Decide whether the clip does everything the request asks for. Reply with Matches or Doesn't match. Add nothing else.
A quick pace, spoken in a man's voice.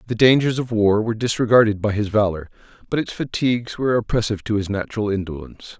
Doesn't match